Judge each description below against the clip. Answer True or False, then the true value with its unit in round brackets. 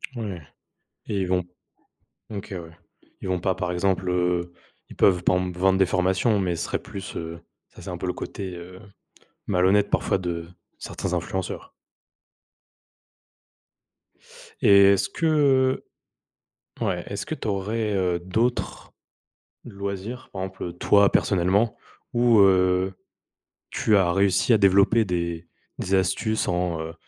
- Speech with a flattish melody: True (2.2 semitones)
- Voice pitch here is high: False (95 Hz)